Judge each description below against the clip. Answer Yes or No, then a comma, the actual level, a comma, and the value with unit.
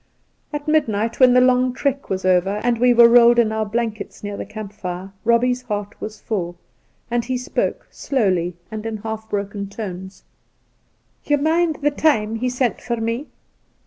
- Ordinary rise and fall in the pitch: Yes, average, 3.5 semitones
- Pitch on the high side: Yes, high, 225 Hz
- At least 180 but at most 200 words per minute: Yes, average, 185 wpm